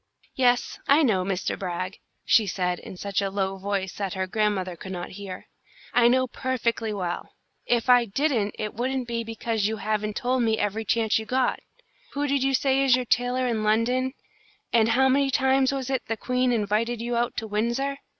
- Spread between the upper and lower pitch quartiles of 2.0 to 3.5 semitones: No, average, 4.0 semitones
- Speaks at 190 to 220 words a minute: Yes, average, 195 wpm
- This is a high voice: Yes, high, 230 Hz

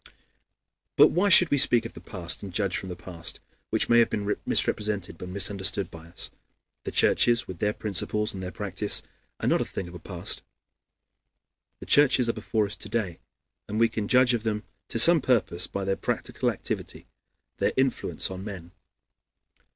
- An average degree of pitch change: Yes, average, 3.8 semitones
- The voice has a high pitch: No, low, 105 Hz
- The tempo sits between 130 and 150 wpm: No, average, 185 wpm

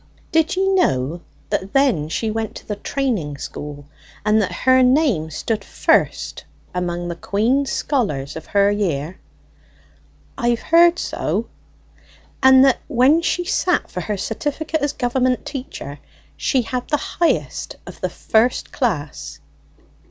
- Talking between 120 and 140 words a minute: Yes, slow, 135 wpm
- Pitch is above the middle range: Yes, high, 225 Hz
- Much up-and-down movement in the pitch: Yes, wide, 7.9 semitones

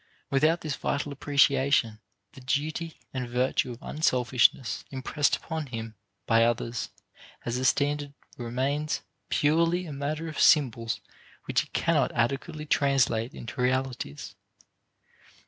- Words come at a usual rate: No, slow, 120 wpm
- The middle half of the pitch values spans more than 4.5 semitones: No, average, 3.5 semitones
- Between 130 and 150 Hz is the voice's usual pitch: Yes, low, 135 Hz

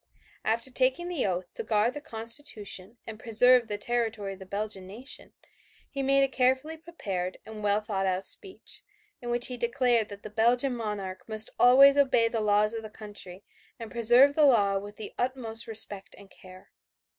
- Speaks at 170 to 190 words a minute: Yes, average, 180 wpm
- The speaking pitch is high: Yes, high, 225 Hz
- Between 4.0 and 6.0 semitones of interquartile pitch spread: No, average, 3.6 semitones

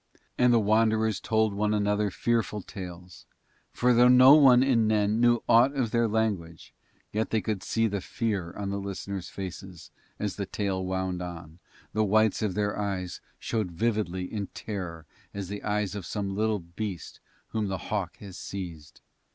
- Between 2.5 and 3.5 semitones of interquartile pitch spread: Yes, average, 2.9 semitones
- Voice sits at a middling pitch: No, low, 105 Hz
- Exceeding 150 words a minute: Yes, average, 175 wpm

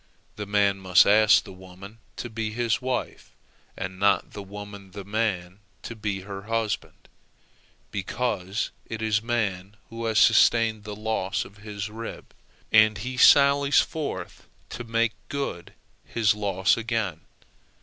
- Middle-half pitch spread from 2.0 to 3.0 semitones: Yes, narrow, 2.6 semitones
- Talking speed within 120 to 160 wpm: Yes, average, 140 wpm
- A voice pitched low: Yes, low, 105 Hz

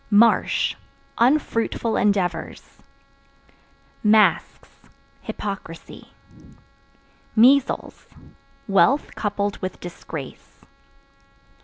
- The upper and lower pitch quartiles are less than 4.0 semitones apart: Yes, average, 3.6 semitones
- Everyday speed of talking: No, slow, 50 wpm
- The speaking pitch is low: No, high, 205 Hz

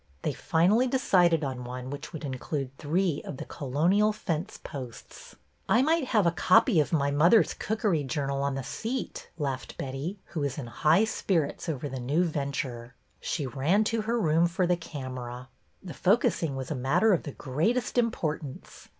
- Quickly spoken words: No, average, 175 wpm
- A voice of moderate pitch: Yes, medium, 155 Hz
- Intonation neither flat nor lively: No, wide, 5.9 semitones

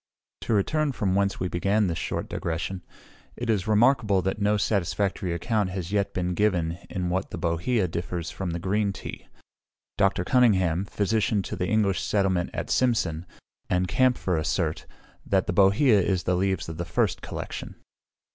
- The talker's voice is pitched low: Yes, very low, 95 Hz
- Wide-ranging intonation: No, average, 2.9 semitones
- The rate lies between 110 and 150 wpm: No, average, 165 wpm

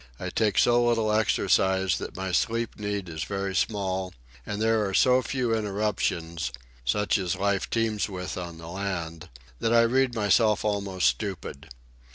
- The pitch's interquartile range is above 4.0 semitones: No, average, 3.2 semitones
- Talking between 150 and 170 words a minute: Yes, average, 160 wpm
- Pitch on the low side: Yes, low, 100 Hz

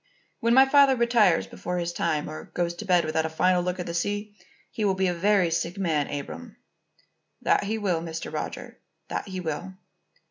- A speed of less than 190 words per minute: No, fast, 205 wpm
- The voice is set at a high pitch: No, medium, 180 Hz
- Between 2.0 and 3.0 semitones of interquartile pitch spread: No, average, 3.7 semitones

